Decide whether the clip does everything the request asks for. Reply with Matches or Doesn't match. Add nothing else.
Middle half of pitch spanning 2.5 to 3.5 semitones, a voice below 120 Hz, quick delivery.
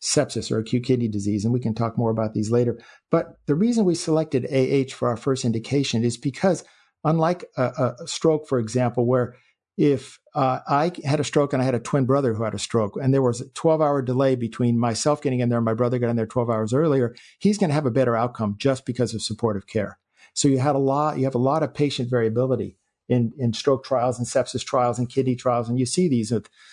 Doesn't match